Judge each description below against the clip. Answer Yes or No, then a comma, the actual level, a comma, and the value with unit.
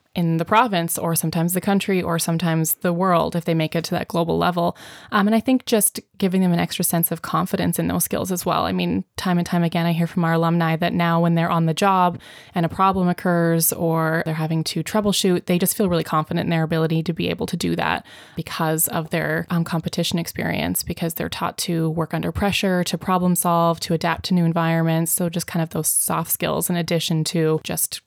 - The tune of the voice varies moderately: No, narrow, 1.5 semitones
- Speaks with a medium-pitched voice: Yes, medium, 170 Hz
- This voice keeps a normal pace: No, fast, 235 wpm